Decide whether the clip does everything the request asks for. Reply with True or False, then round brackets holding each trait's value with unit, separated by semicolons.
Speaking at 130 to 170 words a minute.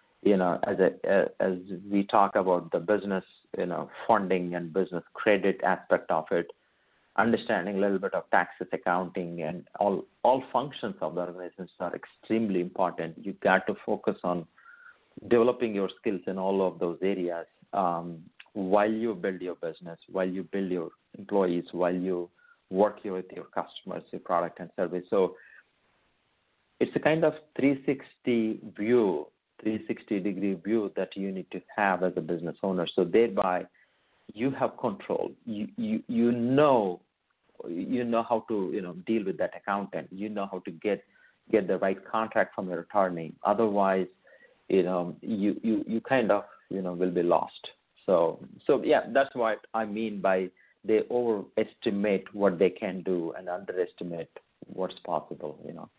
True (165 wpm)